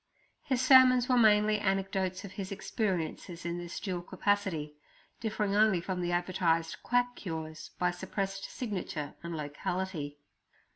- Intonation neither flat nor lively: Yes, average, 3.6 semitones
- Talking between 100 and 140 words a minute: Yes, slow, 135 wpm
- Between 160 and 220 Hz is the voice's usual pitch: Yes, high, 190 Hz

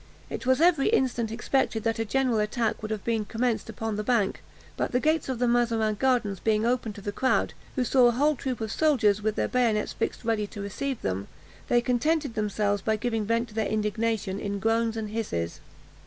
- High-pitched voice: Yes, high, 225 Hz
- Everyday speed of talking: No, fast, 210 wpm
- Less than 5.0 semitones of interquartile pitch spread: Yes, average, 2.8 semitones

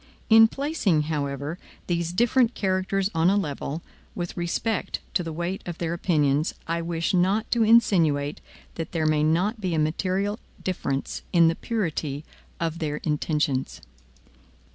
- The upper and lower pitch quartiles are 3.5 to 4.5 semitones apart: Yes, average, 4.0 semitones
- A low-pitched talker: No, medium, 170 Hz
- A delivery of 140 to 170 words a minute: Yes, average, 145 wpm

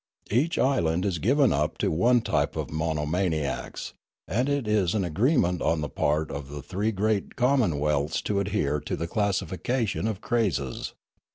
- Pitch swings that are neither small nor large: No, wide, 6.4 semitones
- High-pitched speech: No, very low, 95 Hz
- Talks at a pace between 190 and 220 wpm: No, average, 160 wpm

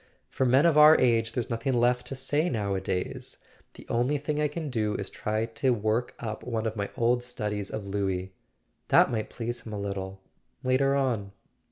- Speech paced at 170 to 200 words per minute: Yes, average, 195 wpm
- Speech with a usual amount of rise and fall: Yes, average, 3.8 semitones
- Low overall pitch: Yes, low, 115 Hz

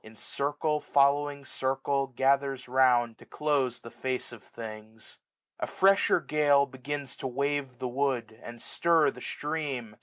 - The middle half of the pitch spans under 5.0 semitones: Yes, average, 2.8 semitones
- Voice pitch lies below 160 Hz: Yes, low, 135 Hz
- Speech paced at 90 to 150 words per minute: Yes, average, 145 wpm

